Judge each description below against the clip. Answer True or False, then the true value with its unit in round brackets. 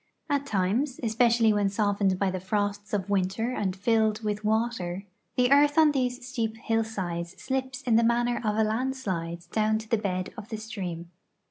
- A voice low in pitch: False (220 Hz)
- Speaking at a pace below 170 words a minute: False (175 wpm)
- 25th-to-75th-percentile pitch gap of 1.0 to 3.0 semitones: False (3.4 semitones)